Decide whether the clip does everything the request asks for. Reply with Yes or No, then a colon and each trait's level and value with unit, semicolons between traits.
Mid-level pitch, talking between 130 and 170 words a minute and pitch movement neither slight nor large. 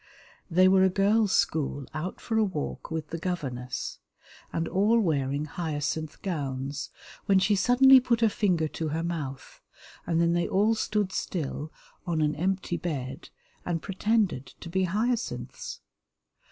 Yes: medium, 175 Hz; average, 150 wpm; average, 4.5 semitones